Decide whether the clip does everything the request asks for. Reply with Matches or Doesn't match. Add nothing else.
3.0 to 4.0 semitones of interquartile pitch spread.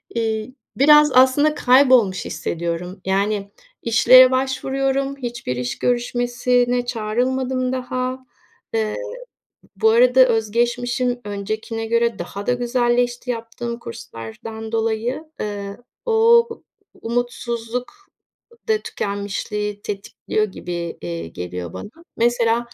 Matches